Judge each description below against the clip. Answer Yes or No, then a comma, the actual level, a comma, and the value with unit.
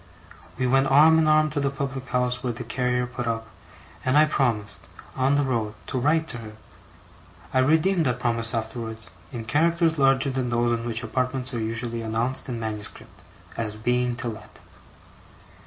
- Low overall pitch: Yes, low, 125 Hz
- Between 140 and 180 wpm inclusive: Yes, average, 175 wpm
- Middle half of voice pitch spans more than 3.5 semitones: No, average, 2.9 semitones